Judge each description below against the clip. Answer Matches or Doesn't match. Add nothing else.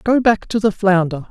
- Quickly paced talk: Matches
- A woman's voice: Doesn't match